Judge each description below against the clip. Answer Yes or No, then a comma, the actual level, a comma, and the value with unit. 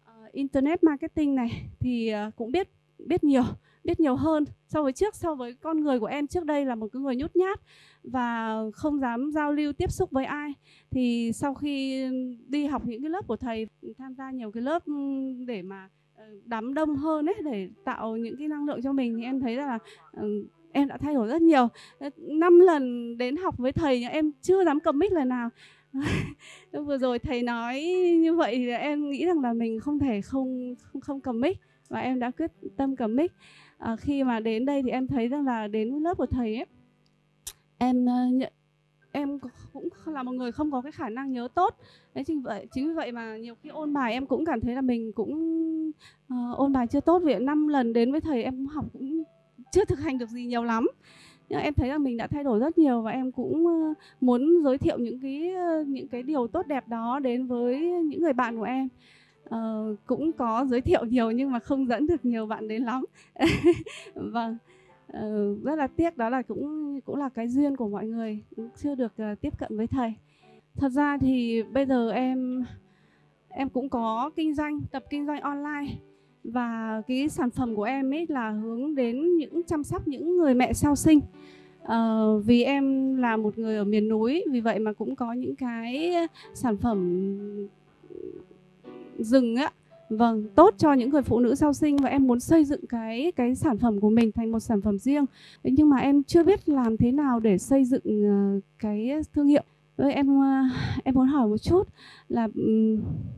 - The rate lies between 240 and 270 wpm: No, average, 200 wpm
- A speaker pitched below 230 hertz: No, very high, 260 Hz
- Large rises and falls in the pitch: No, average, 4.2 semitones